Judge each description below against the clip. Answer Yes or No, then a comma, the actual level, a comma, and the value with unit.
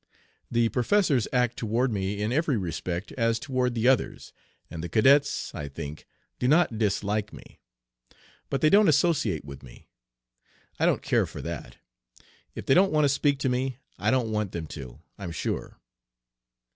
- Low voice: Yes, low, 115 Hz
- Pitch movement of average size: No, wide, 5.7 semitones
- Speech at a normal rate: Yes, average, 170 wpm